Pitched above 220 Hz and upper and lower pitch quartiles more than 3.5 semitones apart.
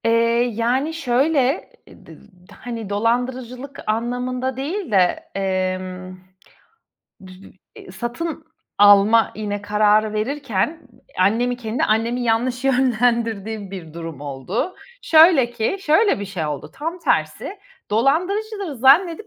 Yes: high, 235 Hz; average, 4.9 semitones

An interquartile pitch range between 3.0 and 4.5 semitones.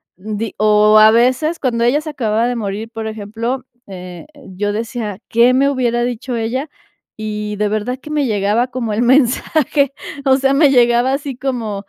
Yes: average, 3.5 semitones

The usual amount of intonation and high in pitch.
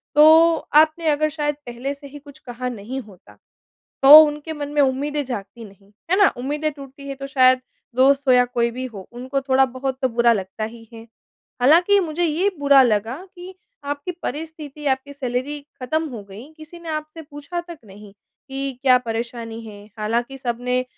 Yes: average, 3.8 semitones; very high, 270 Hz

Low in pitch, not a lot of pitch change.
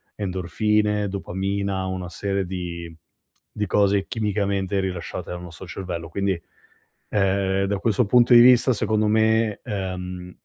Yes: low, 100 Hz; narrow, 2.3 semitones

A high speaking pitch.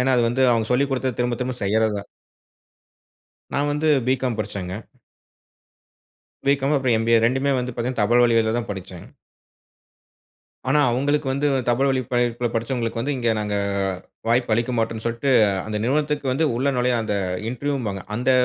No: low, 120 Hz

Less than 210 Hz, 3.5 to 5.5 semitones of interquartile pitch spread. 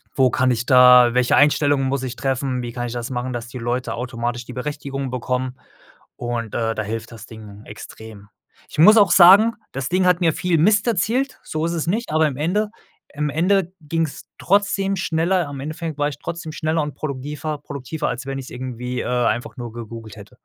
Yes: low, 135 Hz; average, 4.9 semitones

